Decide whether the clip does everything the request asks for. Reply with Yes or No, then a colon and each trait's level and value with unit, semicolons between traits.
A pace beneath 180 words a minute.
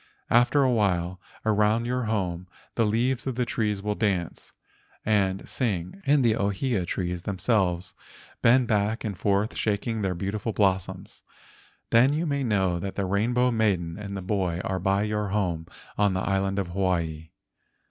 Yes: average, 165 wpm